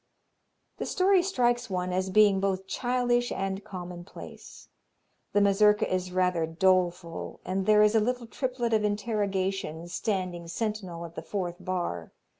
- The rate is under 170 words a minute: Yes, average, 140 wpm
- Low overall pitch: No, high, 195 Hz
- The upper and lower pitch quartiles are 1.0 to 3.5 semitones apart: Yes, average, 3.1 semitones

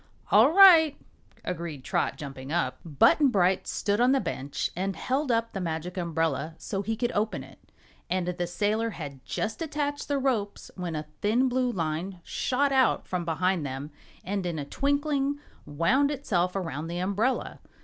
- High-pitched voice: Yes, high, 195 Hz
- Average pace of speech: Yes, average, 170 wpm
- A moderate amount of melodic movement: No, wide, 7.7 semitones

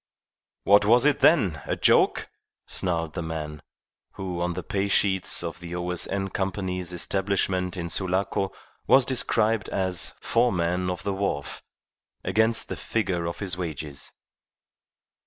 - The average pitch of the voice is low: Yes, very low, 95 Hz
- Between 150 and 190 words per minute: No, slow, 135 wpm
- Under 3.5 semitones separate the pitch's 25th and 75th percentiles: Yes, narrow, 2.4 semitones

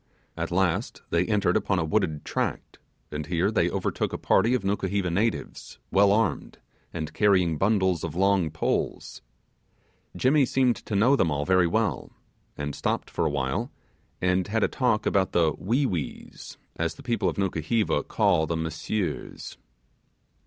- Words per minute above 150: Yes, average, 160 wpm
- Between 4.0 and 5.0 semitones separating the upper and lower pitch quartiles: Yes, average, 4.3 semitones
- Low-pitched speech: Yes, very low, 95 Hz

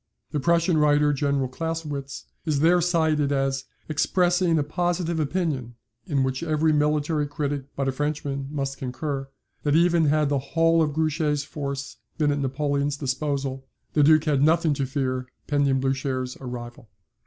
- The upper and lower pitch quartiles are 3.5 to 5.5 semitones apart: No, narrow, 2.5 semitones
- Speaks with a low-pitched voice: No, medium, 145 Hz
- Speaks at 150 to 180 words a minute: Yes, average, 155 wpm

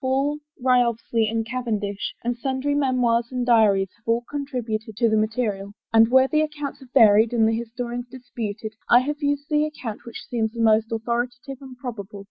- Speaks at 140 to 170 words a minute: No, average, 195 wpm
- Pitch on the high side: Yes, high, 240 Hz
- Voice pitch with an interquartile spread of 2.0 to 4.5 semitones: Yes, average, 2.8 semitones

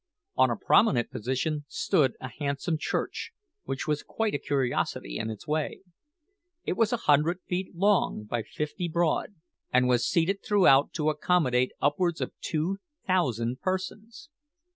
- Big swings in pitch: Yes, wide, 6.0 semitones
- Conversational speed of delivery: Yes, average, 145 wpm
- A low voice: No, medium, 155 Hz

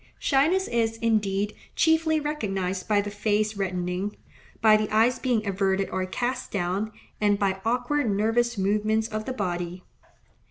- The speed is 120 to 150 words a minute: Yes, average, 145 wpm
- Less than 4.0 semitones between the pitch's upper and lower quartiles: Yes, average, 3.5 semitones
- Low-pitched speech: No, high, 215 Hz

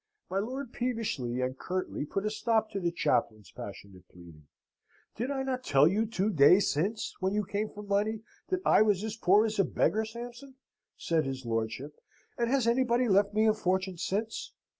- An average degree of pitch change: No, wide, 6.1 semitones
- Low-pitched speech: No, high, 205 Hz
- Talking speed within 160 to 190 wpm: Yes, average, 185 wpm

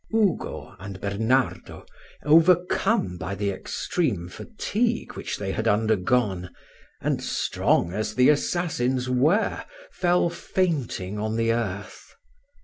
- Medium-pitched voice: No, low, 120 Hz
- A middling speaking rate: No, slow, 110 wpm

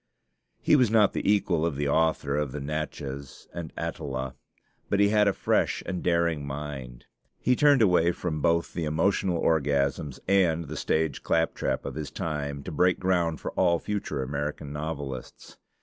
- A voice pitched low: Yes, very low, 80 Hz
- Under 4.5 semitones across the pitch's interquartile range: Yes, average, 3.9 semitones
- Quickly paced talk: No, average, 165 wpm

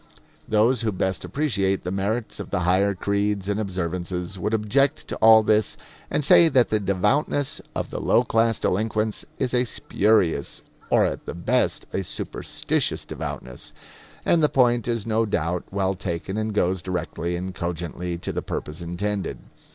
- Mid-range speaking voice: No, low, 100 Hz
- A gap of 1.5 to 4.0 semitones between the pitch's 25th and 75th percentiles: Yes, average, 3.6 semitones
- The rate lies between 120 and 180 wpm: Yes, average, 165 wpm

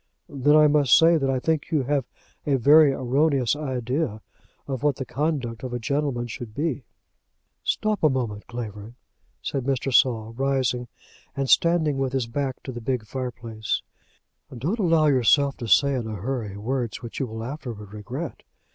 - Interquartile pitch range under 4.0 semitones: Yes, average, 3.5 semitones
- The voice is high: No, low, 130 Hz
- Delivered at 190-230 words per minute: No, average, 170 wpm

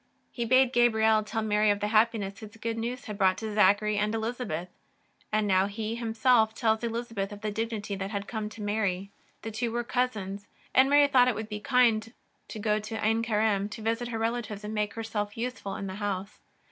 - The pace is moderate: No, fast, 210 wpm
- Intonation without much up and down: Yes, narrow, 1.9 semitones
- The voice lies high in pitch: Yes, high, 220 Hz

